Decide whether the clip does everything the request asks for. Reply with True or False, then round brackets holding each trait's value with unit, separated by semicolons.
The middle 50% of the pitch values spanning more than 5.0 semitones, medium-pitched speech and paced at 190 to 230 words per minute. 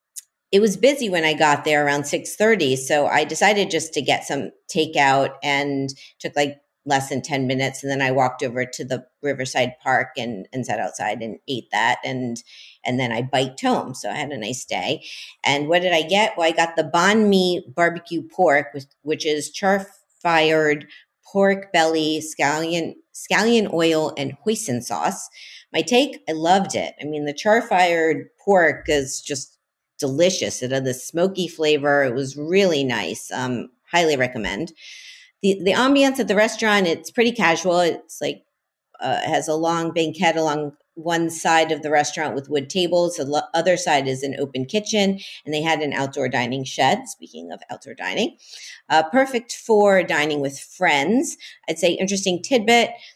False (5.4 semitones; 160 Hz; 175 wpm)